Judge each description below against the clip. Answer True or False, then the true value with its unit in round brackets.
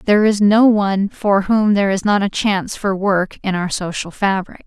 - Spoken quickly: True (220 wpm)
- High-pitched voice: True (200 Hz)